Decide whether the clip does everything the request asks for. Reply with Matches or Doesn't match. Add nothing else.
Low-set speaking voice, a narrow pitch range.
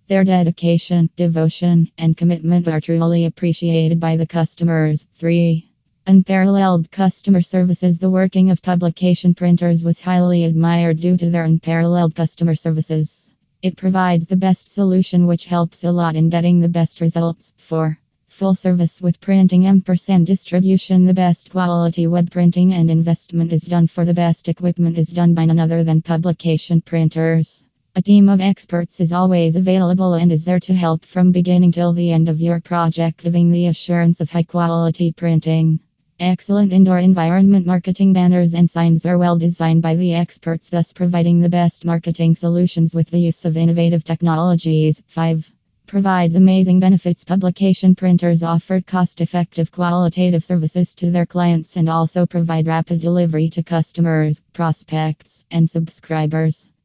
Doesn't match